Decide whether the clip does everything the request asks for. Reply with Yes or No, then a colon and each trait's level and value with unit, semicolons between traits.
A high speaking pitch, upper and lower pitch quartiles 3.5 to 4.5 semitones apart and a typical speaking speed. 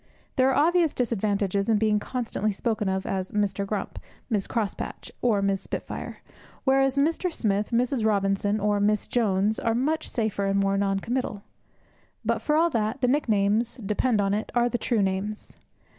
Yes: high, 215 Hz; average, 3.8 semitones; average, 170 wpm